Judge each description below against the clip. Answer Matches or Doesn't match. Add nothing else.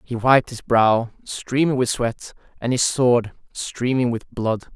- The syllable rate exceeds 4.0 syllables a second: Doesn't match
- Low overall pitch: Matches